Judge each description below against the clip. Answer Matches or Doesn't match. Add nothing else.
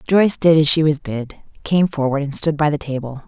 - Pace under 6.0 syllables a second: Matches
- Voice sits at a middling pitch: Matches